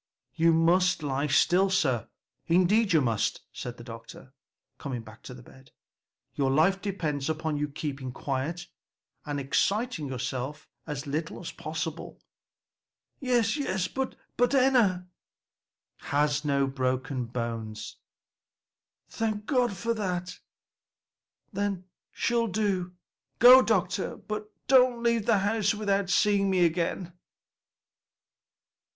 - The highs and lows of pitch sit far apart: Yes, wide, 6.9 semitones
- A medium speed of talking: No, slow, 115 wpm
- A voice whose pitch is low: No, medium, 175 Hz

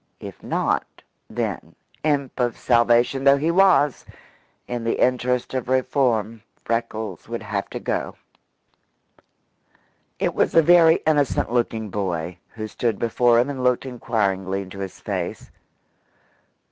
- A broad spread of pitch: No, average, 3.6 semitones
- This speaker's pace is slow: Yes, slow, 130 wpm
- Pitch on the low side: Yes, low, 120 Hz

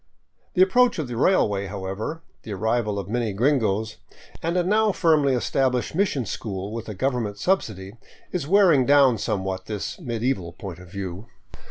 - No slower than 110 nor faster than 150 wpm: No, average, 165 wpm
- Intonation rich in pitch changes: Yes, wide, 6.9 semitones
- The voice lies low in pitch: Yes, low, 115 Hz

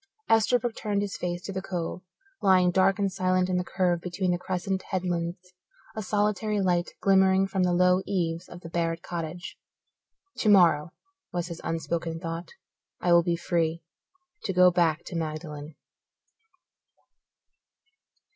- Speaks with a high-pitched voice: No, medium, 180 Hz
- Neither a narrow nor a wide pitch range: No, narrow, 2.1 semitones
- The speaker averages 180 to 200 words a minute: No, average, 145 wpm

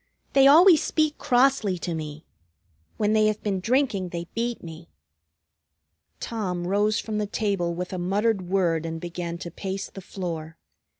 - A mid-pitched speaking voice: No, high, 195 Hz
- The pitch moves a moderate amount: Yes, average, 4.2 semitones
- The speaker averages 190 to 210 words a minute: No, average, 160 wpm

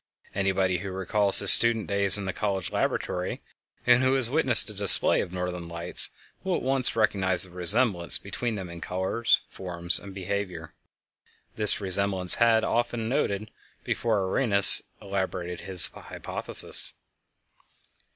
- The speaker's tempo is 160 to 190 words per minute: No, average, 140 wpm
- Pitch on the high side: No, low, 100 Hz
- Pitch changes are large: No, average, 3.4 semitones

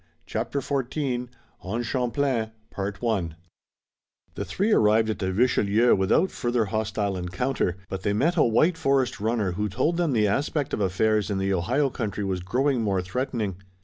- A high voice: No, low, 110 Hz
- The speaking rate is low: No, average, 155 wpm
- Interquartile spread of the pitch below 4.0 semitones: No, average, 4.9 semitones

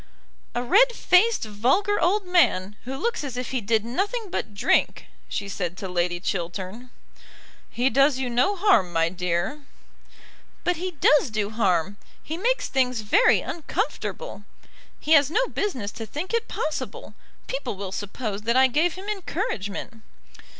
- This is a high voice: Yes, very high, 255 Hz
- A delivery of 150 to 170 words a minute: Yes, average, 155 wpm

